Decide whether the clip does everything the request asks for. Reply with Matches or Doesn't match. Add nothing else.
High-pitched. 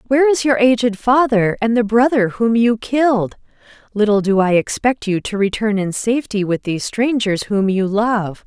Matches